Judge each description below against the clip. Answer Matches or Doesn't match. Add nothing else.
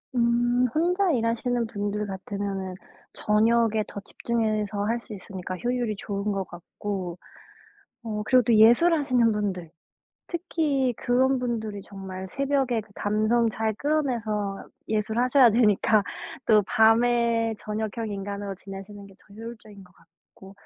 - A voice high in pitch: Matches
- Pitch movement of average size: Matches